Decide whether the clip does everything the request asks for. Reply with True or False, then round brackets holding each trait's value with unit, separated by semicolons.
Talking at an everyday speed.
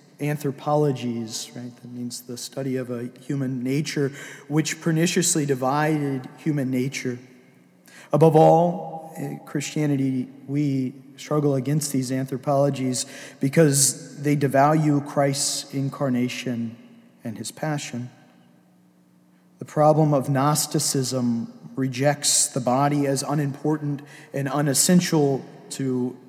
False (100 wpm)